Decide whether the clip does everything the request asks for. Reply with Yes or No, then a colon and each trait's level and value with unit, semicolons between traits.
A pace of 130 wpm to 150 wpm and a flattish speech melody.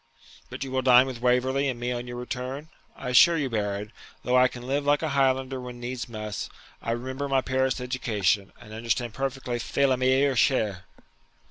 No: average, 195 wpm; narrow, 1.9 semitones